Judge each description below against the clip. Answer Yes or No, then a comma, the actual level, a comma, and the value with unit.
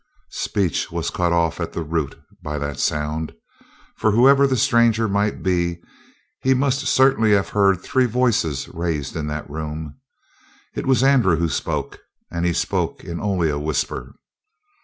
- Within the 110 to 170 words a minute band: Yes, average, 160 wpm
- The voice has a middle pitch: No, very low, 85 Hz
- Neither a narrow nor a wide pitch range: No, wide, 6.8 semitones